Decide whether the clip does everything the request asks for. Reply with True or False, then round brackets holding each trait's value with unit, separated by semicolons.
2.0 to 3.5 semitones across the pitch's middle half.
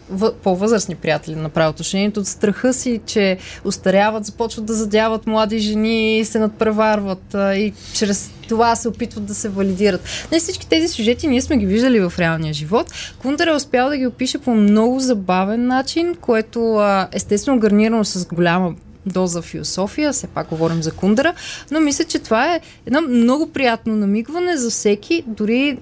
False (4.2 semitones)